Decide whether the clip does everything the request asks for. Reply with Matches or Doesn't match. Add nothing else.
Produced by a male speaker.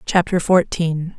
Doesn't match